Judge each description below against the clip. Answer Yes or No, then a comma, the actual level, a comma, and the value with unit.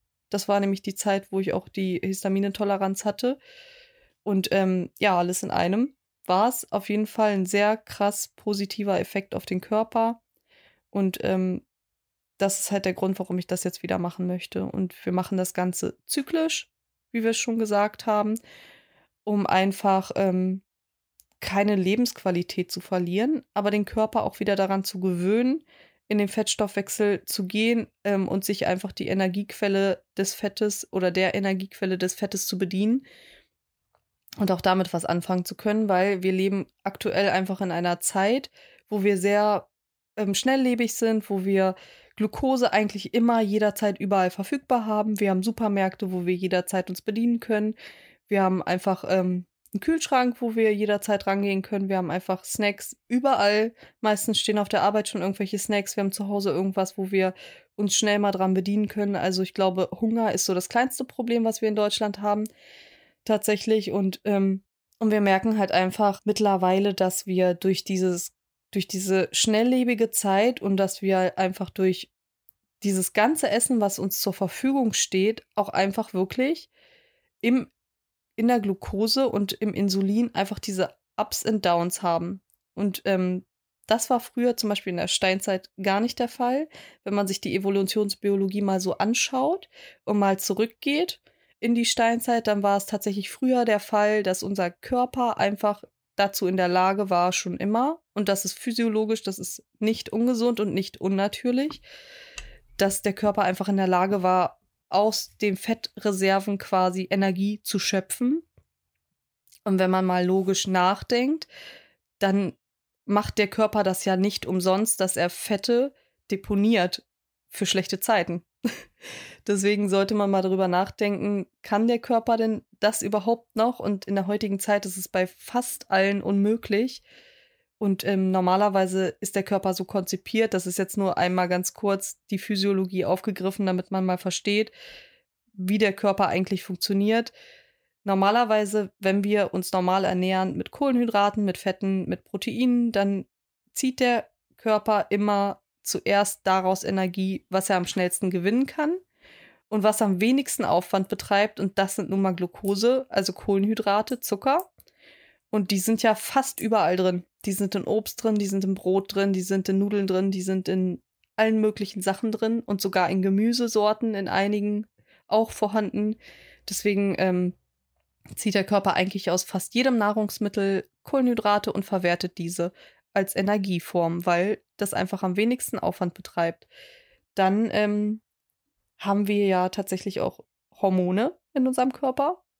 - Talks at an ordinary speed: Yes, average, 160 wpm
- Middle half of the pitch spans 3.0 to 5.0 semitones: No, narrow, 2.5 semitones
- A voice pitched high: Yes, high, 200 Hz